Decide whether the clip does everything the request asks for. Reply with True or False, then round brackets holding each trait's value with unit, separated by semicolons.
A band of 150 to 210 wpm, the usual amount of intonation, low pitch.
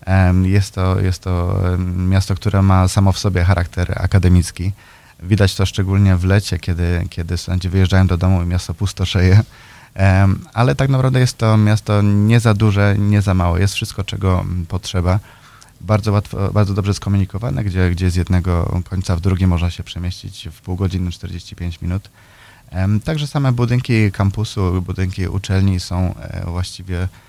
False (155 wpm; 2.2 semitones; 95 Hz)